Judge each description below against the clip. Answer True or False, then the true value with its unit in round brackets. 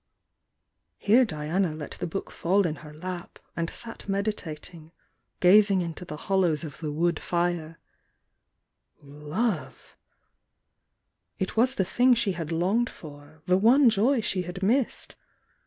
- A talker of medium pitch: True (180 Hz)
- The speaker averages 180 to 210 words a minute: False (135 wpm)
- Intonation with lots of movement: False (4.7 semitones)